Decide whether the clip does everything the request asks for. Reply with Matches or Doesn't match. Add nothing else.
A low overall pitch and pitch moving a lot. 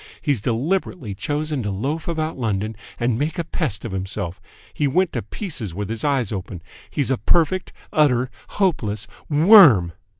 Matches